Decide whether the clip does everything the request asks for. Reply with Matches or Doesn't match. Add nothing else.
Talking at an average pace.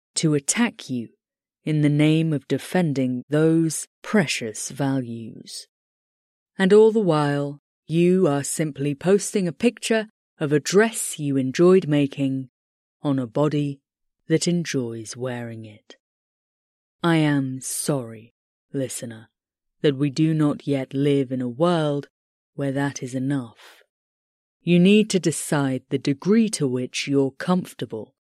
Doesn't match